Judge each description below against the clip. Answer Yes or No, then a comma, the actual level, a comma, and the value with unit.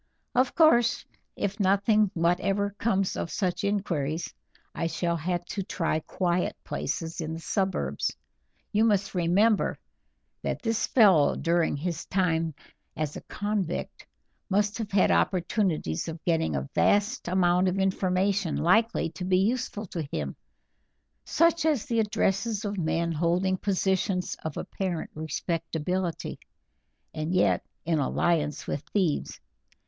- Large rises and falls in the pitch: No, average, 3.4 semitones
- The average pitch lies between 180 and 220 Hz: Yes, medium, 185 Hz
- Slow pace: Yes, slow, 130 wpm